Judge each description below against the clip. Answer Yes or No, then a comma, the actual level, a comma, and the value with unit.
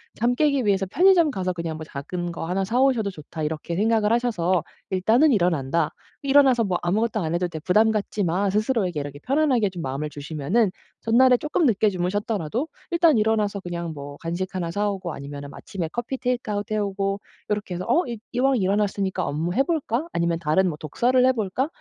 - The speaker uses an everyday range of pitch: No, wide, 5.7 semitones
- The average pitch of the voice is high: Yes, high, 200 Hz